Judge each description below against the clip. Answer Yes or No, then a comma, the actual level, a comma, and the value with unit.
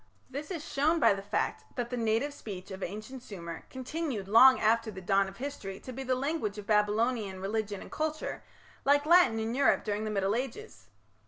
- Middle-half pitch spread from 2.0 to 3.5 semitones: No, average, 5.0 semitones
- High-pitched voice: Yes, high, 225 Hz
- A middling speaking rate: Yes, average, 195 wpm